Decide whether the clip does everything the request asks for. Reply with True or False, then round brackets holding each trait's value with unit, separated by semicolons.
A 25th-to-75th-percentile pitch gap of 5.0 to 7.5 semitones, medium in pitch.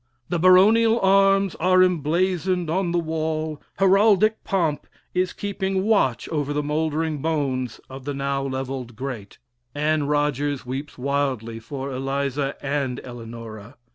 True (5.3 semitones; 150 Hz)